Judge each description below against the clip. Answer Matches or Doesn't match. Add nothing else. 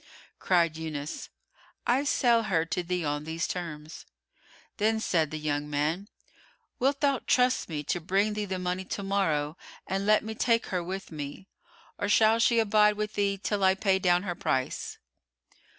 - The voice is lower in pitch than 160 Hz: Doesn't match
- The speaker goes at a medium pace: Matches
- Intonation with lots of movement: Doesn't match